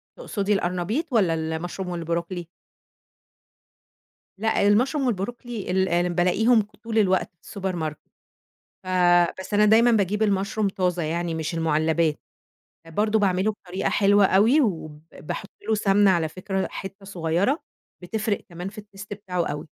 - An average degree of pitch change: Yes, average, 3.4 semitones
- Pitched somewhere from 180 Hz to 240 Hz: Yes, high, 190 Hz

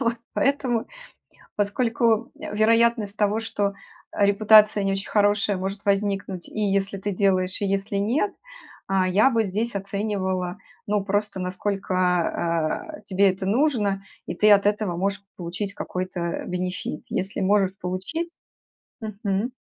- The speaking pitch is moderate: No, high, 200 Hz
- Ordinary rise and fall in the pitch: No, narrow, 2.0 semitones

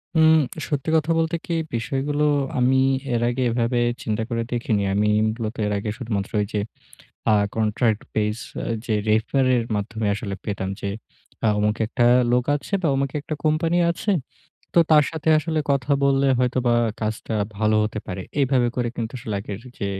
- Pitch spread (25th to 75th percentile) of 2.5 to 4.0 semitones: No, average, 4.4 semitones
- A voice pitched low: Yes, low, 120 Hz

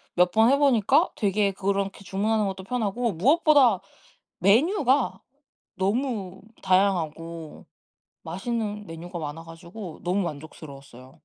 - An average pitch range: Yes, average, 4.7 semitones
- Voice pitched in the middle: No, high, 195 Hz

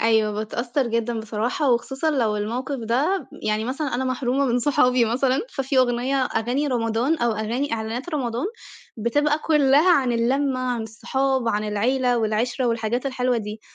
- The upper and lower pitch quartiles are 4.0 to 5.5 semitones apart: No, average, 2.9 semitones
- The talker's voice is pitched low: No, high, 245 Hz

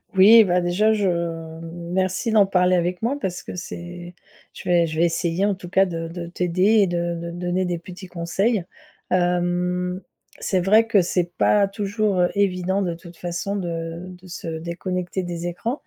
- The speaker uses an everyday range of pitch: No, narrow, 1.9 semitones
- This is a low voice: No, medium, 180 Hz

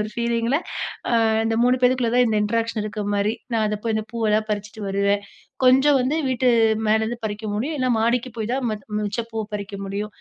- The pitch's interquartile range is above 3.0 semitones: No, narrow, 2.6 semitones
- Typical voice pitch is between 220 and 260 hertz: Yes, high, 225 Hz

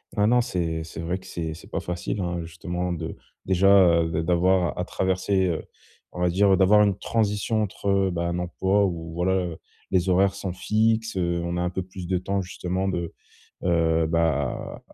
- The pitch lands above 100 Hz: No, very low, 90 Hz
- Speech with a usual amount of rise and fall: No, narrow, 2.1 semitones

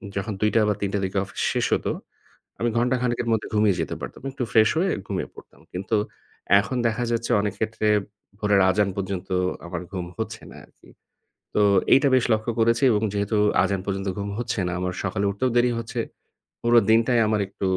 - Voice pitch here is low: Yes, low, 105 Hz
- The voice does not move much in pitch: No, average, 3.0 semitones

